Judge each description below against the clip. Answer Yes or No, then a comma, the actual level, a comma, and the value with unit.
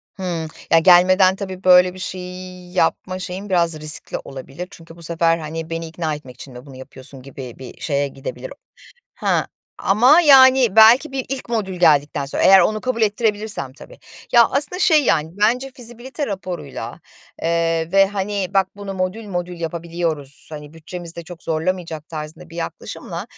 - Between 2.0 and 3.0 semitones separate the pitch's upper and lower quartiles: No, average, 4.1 semitones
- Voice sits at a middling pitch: Yes, medium, 180 Hz